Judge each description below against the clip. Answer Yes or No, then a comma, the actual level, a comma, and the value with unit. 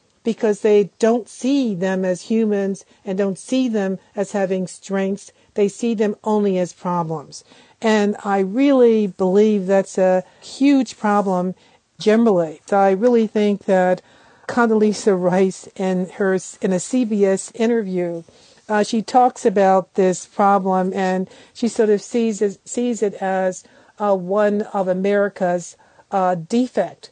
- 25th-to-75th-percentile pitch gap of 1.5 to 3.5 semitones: Yes, average, 3.0 semitones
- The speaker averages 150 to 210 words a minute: No, slow, 135 wpm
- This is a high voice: Yes, high, 200 Hz